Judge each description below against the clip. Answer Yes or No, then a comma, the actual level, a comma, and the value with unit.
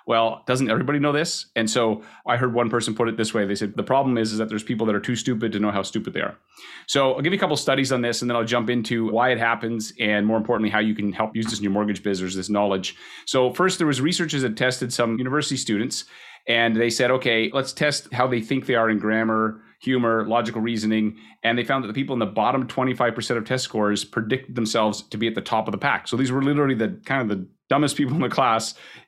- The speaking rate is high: Yes, fast, 265 wpm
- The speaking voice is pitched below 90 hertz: No, low, 115 Hz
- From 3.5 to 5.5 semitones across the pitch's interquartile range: No, average, 2.8 semitones